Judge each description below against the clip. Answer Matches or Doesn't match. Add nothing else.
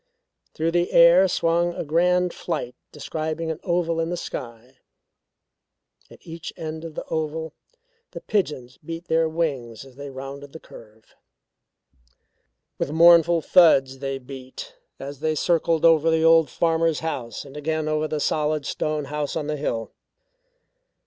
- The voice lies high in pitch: Doesn't match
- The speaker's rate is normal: Matches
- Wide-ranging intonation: Doesn't match